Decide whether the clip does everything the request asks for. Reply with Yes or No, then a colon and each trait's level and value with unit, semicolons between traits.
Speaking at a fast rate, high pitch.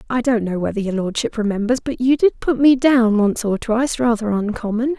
Yes: fast, 215 wpm; high, 230 Hz